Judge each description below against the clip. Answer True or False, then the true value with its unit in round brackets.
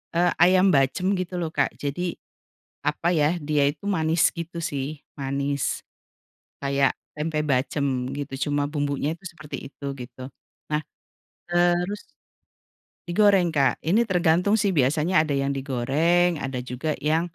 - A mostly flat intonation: False (3.9 semitones)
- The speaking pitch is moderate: True (155 Hz)